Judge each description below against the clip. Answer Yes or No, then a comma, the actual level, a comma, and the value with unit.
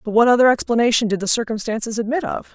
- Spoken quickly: Yes, fast, 210 wpm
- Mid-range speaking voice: No, high, 230 Hz